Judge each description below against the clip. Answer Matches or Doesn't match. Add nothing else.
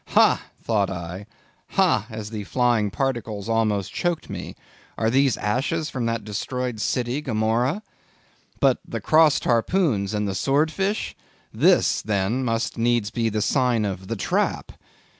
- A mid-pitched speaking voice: Doesn't match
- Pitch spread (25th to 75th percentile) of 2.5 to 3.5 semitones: Doesn't match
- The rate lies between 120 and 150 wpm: Matches